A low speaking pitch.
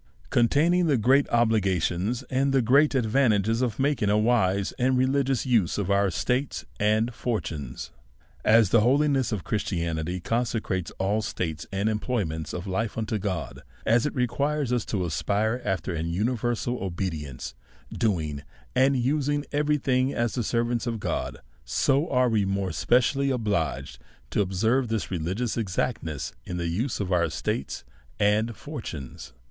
Yes: low, 110 Hz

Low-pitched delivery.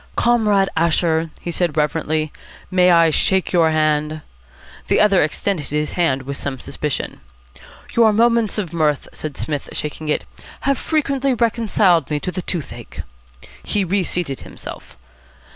No: medium, 170 Hz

